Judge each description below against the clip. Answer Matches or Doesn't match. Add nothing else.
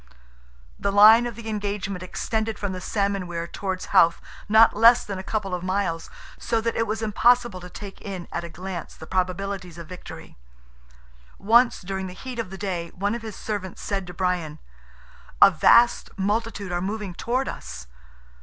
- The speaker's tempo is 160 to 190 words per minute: Matches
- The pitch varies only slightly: Doesn't match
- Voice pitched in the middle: Doesn't match